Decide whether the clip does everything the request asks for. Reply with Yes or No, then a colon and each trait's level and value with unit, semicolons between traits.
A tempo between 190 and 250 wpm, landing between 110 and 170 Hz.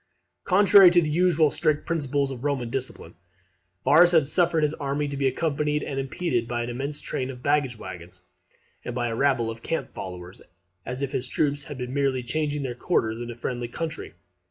Yes: average, 200 wpm; medium, 140 Hz